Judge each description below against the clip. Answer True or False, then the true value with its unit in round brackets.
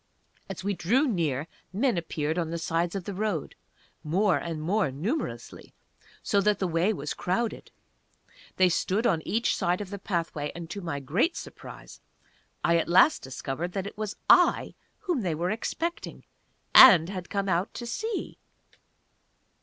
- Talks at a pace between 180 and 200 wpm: False (160 wpm)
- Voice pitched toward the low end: False (185 Hz)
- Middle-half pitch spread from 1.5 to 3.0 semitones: False (4.2 semitones)